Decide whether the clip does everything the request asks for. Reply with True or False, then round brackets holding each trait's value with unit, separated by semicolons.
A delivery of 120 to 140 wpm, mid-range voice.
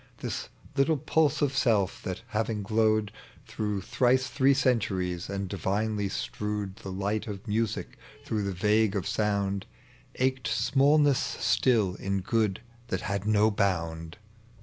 False (135 wpm; 105 Hz)